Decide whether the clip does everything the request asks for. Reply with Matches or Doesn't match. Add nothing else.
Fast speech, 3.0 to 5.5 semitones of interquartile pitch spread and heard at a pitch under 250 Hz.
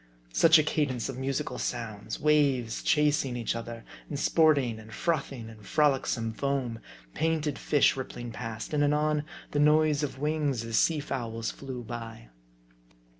Doesn't match